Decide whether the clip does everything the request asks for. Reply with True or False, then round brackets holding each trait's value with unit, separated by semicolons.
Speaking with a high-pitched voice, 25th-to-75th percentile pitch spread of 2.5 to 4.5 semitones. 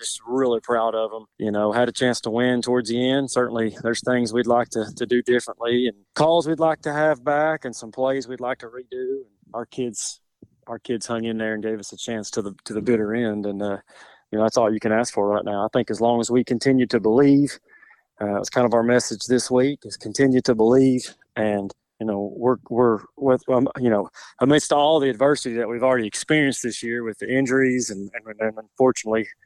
False (120 Hz; 2.8 semitones)